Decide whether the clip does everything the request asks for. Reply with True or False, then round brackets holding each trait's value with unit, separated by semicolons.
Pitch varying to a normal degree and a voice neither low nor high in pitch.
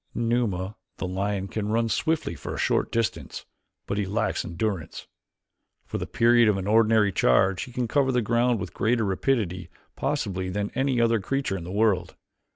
False (3.7 semitones; 105 Hz)